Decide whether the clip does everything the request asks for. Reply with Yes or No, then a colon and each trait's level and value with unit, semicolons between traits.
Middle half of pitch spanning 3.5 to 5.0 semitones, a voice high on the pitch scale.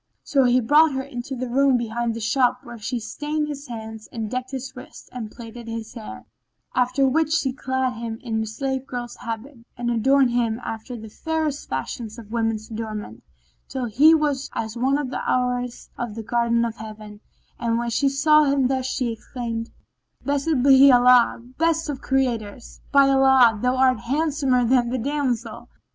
No: average, 2.9 semitones; very high, 250 Hz